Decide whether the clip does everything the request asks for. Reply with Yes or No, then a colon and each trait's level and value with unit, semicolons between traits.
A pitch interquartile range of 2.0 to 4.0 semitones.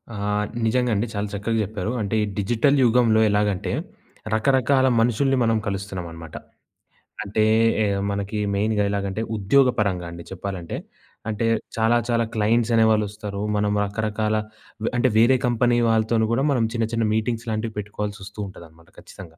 Yes: narrow, 2.5 semitones